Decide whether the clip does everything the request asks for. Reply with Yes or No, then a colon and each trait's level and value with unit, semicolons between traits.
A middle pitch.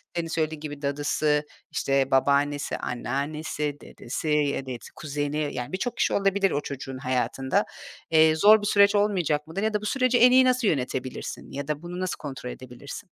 Yes: medium, 150 Hz